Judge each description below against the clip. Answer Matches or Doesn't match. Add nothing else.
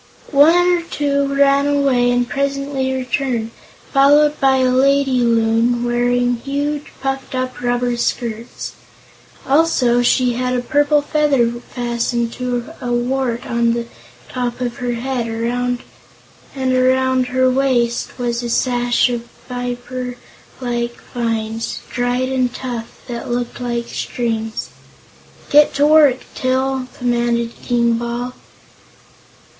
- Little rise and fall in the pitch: Matches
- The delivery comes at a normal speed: Doesn't match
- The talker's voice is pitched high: Matches